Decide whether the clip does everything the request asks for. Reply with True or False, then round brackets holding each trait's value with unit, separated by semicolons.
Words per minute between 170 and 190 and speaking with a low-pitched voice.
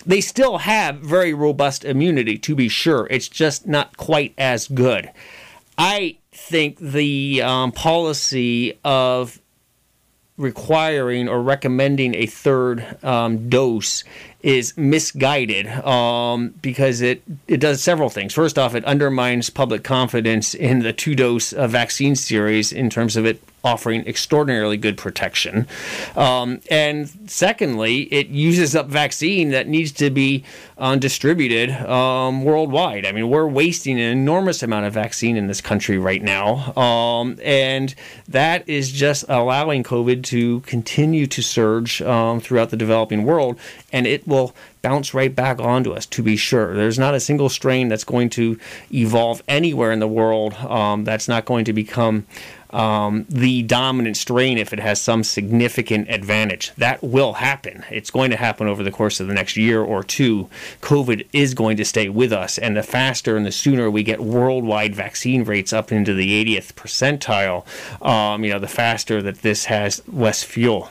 False (160 wpm; 125 Hz)